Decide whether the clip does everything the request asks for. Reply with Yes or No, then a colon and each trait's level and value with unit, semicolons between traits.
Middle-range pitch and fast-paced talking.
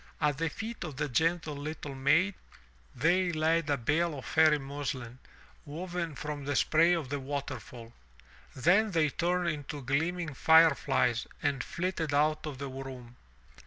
No: medium, 150 Hz; average, 155 wpm